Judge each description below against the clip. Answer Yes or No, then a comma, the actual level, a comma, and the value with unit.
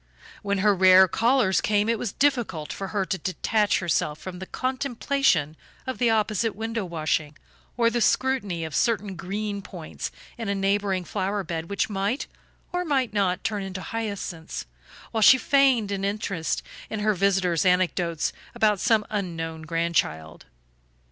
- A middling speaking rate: Yes, average, 155 wpm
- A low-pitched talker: No, high, 200 Hz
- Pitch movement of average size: Yes, average, 3.8 semitones